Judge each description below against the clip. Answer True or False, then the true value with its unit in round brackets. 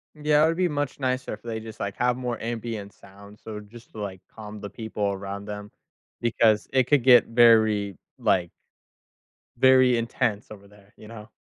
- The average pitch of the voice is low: True (110 Hz)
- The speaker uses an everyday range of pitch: True (3.1 semitones)